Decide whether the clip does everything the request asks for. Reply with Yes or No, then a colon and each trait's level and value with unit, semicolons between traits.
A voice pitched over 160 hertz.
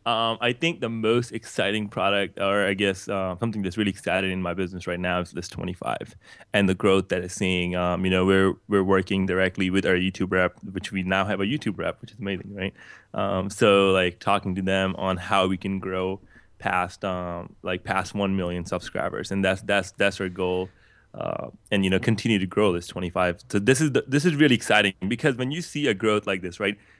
No: very low, 95 Hz